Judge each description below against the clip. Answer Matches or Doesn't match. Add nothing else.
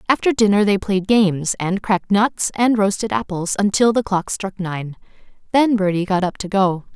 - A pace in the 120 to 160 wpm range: Doesn't match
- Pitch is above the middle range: Matches